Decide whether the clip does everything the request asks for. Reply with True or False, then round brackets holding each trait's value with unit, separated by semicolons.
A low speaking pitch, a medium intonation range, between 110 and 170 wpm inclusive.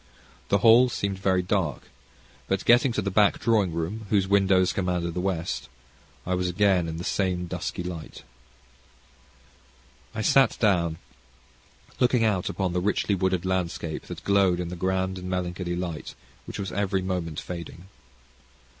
False (95 Hz; 2.2 semitones; 155 wpm)